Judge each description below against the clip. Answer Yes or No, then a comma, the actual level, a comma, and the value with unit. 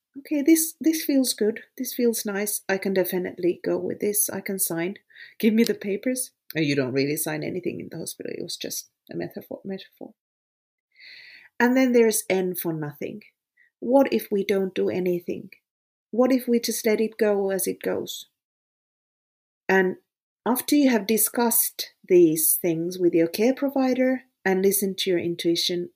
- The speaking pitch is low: No, high, 220 Hz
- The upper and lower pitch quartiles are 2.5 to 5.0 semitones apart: No, wide, 5.6 semitones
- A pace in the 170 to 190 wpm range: Yes, average, 175 wpm